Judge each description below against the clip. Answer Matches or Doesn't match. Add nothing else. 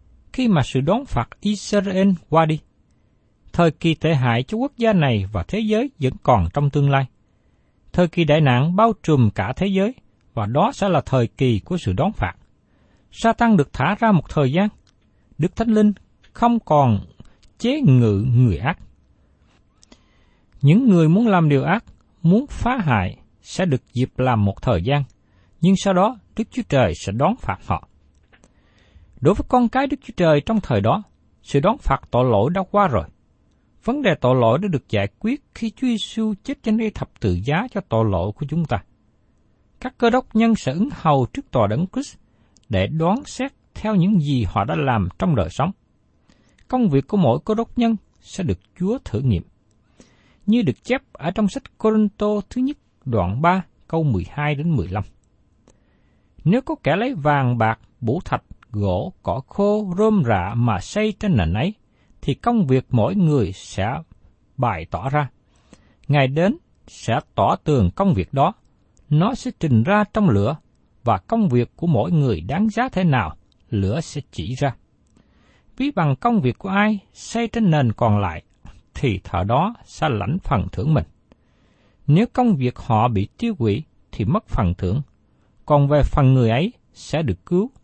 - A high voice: Doesn't match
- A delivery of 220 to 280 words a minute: Doesn't match